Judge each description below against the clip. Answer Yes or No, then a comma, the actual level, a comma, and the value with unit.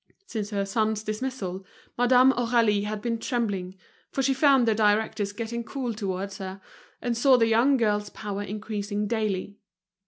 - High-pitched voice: Yes, high, 215 Hz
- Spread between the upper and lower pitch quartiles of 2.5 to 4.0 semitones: Yes, average, 2.8 semitones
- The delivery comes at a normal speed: Yes, average, 155 wpm